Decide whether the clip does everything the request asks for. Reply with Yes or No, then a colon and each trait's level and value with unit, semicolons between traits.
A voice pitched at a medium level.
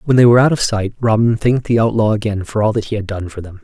No: low, 110 Hz